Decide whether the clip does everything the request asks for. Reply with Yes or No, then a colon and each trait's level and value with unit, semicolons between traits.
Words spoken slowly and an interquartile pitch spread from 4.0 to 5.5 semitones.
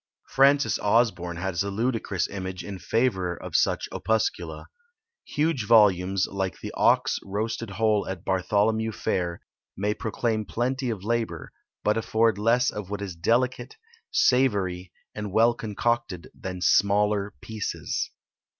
No: slow, 130 wpm; average, 3.3 semitones